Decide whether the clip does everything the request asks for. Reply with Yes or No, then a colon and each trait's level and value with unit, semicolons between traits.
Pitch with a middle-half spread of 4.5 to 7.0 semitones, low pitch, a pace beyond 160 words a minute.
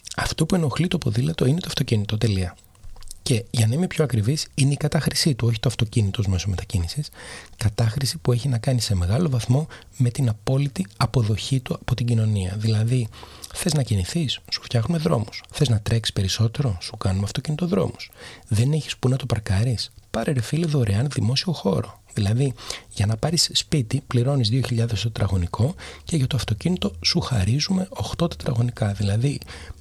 Yes: average, 5.2 semitones; low, 120 Hz; fast, 170 wpm